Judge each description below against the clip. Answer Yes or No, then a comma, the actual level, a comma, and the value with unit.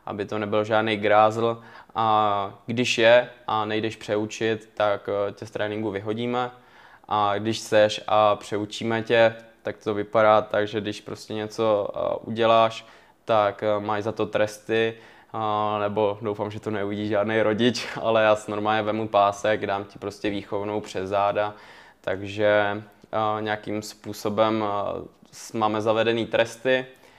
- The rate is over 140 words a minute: No, average, 135 wpm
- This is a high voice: No, low, 105 Hz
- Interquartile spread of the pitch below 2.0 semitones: Yes, narrow, 1.2 semitones